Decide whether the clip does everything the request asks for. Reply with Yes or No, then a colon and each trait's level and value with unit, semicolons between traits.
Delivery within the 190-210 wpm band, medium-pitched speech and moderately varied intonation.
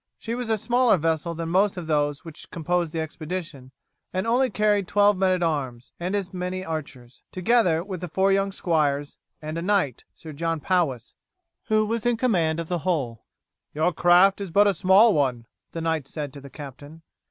Yes: average, 195 wpm; medium, 170 Hz; average, 4.3 semitones